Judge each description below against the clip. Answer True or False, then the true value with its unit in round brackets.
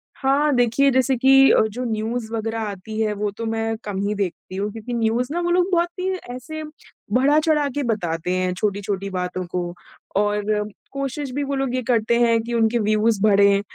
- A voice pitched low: False (225 Hz)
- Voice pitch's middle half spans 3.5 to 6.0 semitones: True (4.5 semitones)